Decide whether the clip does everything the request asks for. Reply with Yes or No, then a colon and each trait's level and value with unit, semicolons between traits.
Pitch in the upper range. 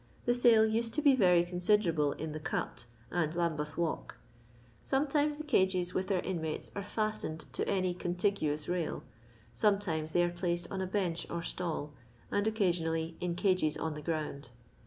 No: medium, 175 Hz